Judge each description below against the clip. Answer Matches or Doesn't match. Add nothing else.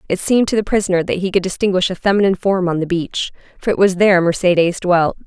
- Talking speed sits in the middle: Doesn't match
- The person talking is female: Matches